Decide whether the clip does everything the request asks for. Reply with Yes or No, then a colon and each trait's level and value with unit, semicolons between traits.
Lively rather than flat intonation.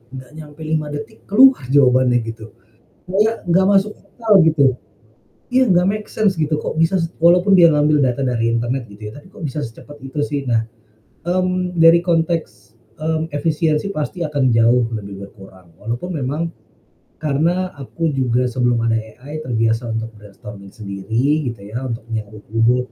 Yes: wide, 6.4 semitones